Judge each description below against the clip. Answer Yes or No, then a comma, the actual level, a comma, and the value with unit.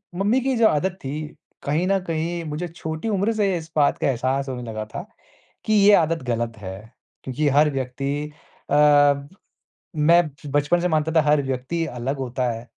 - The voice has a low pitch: No, medium, 150 Hz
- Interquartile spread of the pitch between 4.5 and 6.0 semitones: Yes, average, 4.8 semitones